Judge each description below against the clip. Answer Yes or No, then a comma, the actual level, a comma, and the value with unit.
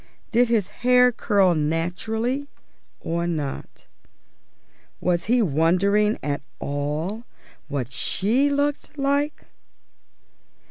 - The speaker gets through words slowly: Yes, slow, 90 wpm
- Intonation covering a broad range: Yes, wide, 7.2 semitones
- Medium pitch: No, high, 200 Hz